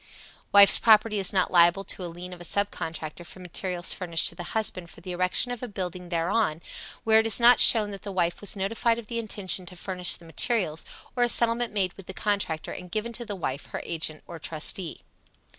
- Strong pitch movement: No, average, 3.8 semitones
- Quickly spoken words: Yes, fast, 225 wpm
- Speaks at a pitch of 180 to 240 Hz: Yes, medium, 185 Hz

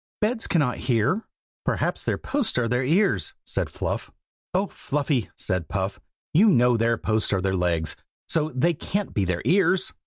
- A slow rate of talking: No, average, 165 wpm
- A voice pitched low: Yes, low, 125 Hz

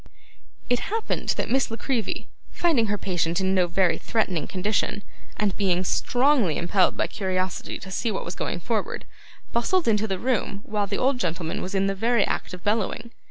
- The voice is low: No, high, 200 Hz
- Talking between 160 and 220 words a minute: Yes, average, 185 wpm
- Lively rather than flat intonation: No, average, 4.0 semitones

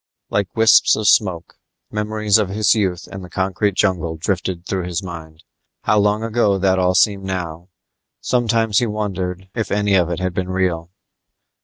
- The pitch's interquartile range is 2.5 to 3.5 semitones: Yes, average, 2.8 semitones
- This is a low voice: Yes, very low, 95 Hz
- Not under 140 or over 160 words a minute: No, average, 170 wpm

